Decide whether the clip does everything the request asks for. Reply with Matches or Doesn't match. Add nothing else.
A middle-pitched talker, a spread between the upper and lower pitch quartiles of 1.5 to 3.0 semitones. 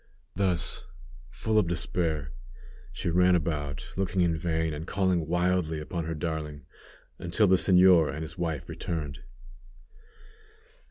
Doesn't match